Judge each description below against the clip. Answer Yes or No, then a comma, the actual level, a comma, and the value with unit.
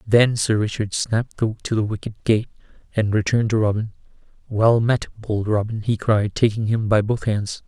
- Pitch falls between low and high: No, low, 110 Hz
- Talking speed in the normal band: Yes, average, 180 wpm